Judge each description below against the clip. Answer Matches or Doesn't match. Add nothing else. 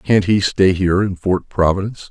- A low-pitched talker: Matches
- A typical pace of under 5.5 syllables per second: Matches